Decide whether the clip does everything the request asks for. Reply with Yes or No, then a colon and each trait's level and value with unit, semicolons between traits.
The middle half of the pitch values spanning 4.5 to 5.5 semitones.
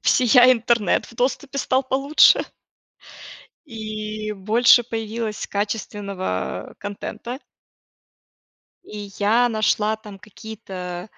No: average, 2.9 semitones